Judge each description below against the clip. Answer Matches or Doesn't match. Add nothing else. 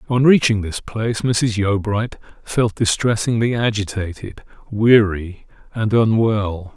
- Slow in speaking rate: Matches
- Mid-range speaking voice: Doesn't match